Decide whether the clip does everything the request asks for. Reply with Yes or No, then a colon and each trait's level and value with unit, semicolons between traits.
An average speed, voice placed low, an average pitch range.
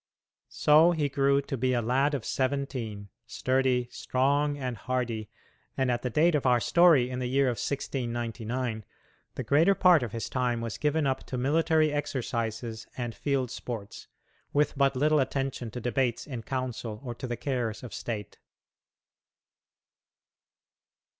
Yes: average, 155 wpm; low, 130 Hz; average, 3.0 semitones